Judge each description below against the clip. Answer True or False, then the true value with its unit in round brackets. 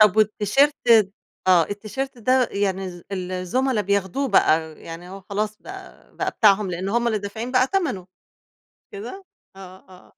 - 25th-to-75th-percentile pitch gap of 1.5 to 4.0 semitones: False (5.2 semitones)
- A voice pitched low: False (205 Hz)